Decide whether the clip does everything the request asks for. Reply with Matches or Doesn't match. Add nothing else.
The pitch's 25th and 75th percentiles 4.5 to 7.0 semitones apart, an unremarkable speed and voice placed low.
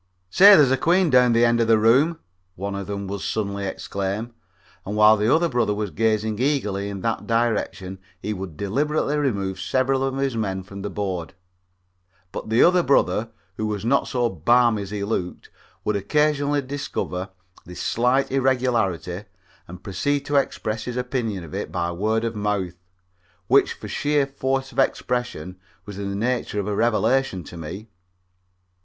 Matches